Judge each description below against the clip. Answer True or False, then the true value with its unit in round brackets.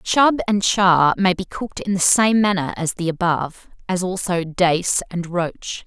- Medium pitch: True (180 Hz)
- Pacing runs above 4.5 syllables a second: False (4.2 syllables/s)